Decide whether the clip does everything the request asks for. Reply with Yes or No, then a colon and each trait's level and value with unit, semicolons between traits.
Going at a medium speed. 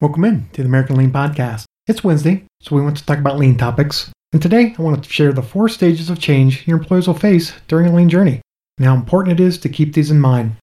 No: fast, 260 wpm